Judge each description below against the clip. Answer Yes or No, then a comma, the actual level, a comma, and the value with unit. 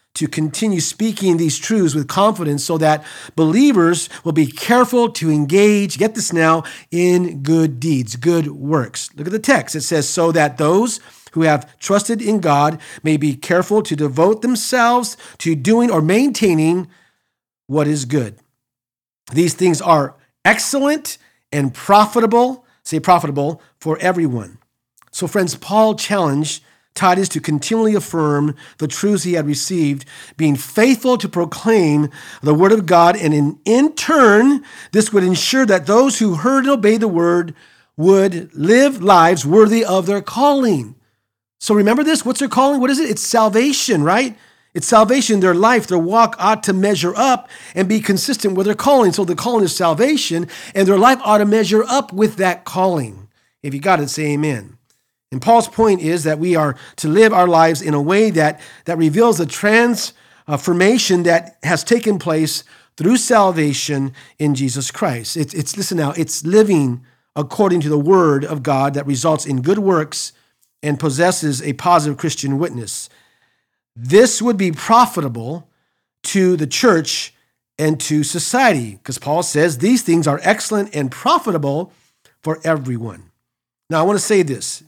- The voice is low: No, medium, 170 Hz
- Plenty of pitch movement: Yes, wide, 6.2 semitones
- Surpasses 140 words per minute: Yes, average, 165 wpm